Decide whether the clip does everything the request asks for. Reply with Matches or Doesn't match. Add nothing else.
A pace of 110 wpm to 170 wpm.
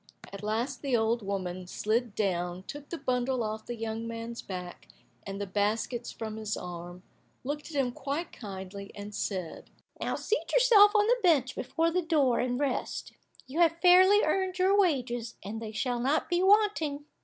Doesn't match